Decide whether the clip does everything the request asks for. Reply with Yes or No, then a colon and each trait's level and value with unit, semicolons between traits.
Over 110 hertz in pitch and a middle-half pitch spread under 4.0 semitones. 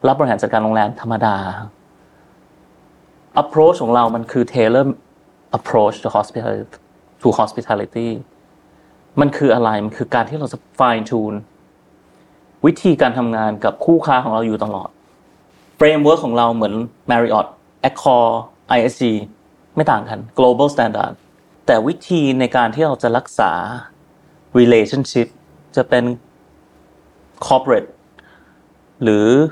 Yes: low, 120 Hz; average, 3.1 semitones